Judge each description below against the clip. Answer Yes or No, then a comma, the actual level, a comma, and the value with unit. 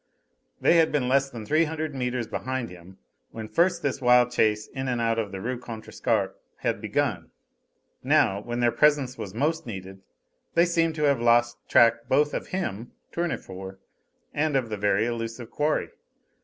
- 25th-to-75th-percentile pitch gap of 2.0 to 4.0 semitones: No, average, 4.7 semitones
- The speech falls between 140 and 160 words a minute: No, average, 170 wpm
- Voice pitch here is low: Yes, low, 120 Hz